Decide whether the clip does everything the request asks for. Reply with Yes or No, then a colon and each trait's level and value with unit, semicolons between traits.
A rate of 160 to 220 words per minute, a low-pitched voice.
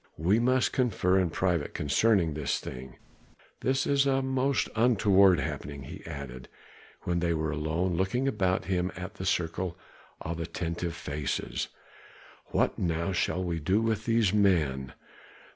No: average, 145 wpm; very low, 90 Hz